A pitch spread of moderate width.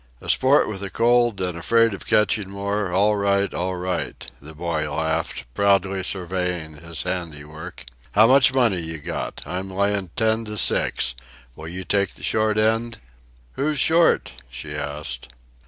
Yes: average, 4.4 semitones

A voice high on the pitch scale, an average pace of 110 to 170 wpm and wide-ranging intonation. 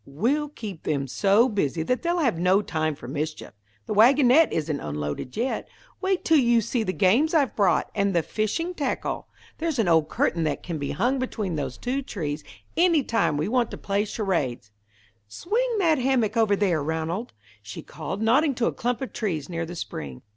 No: high, 205 Hz; average, 190 wpm; wide, 8.5 semitones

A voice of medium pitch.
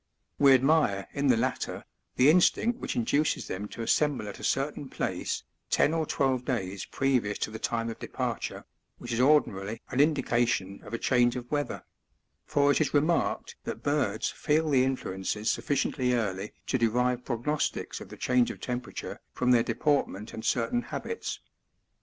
No: low, 125 Hz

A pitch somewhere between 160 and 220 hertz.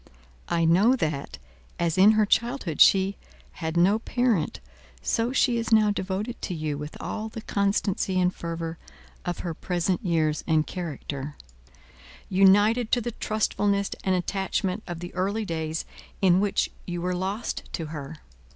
Yes: medium, 185 Hz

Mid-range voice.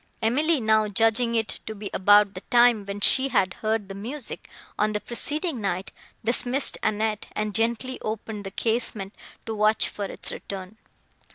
No: high, 220 Hz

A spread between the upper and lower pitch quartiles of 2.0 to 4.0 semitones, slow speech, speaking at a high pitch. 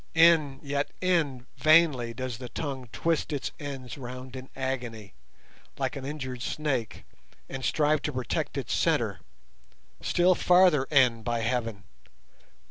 No: average, 3.4 semitones; slow, 130 wpm; low, 135 Hz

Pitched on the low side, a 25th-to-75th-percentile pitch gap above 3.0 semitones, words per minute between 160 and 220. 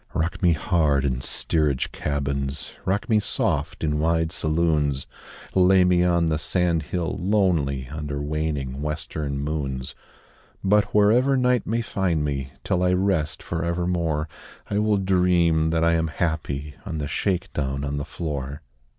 No: very low, 80 Hz; average, 3.9 semitones; average, 150 wpm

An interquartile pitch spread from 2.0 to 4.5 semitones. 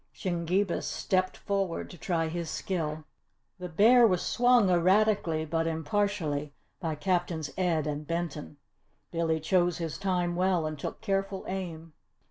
Yes: average, 3.2 semitones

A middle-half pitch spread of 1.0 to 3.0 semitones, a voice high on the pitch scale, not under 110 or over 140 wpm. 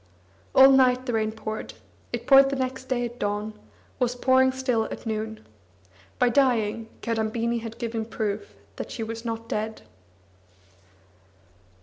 Yes: narrow, 2.6 semitones; high, 230 Hz; slow, 135 wpm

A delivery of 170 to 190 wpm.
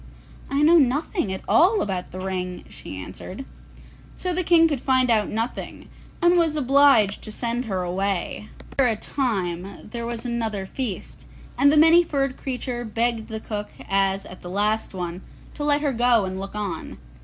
Yes: average, 180 wpm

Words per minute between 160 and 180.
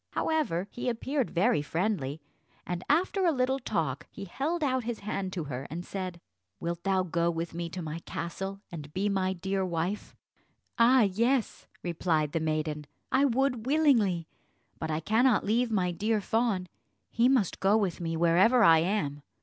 Yes: average, 170 wpm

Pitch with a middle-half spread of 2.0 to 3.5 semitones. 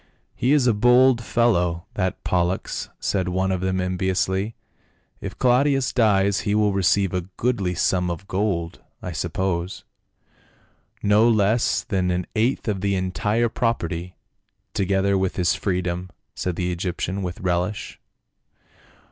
Yes: average, 2.9 semitones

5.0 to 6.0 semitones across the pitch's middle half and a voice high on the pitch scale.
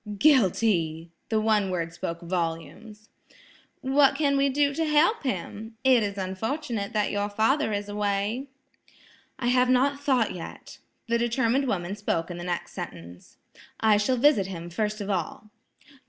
Yes: wide, 5.5 semitones; high, 215 Hz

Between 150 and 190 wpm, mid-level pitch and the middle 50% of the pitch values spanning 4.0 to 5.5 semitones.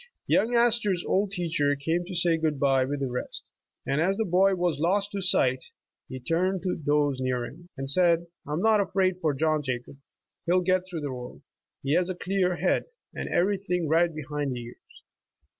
No: fast, 205 wpm; medium, 170 Hz; average, 4.5 semitones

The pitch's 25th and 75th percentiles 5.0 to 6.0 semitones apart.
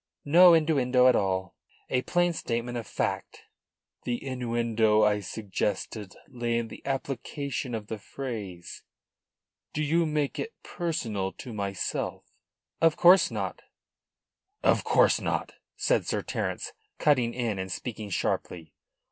Yes: average, 5.3 semitones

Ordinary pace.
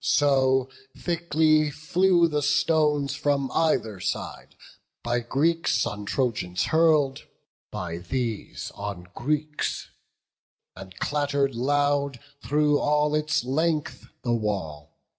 No: slow, 105 wpm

